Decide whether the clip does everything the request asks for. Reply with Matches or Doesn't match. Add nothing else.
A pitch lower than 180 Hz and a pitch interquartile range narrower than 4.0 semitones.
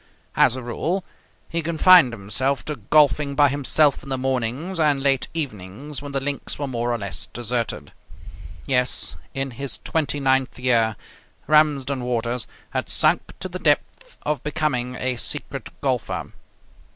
Matches